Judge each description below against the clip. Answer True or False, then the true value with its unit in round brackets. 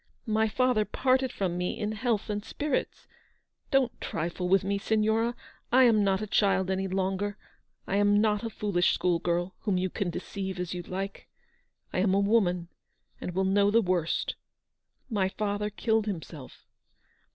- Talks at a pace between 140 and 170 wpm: True (165 wpm)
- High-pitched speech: True (200 Hz)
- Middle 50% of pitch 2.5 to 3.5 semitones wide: True (2.8 semitones)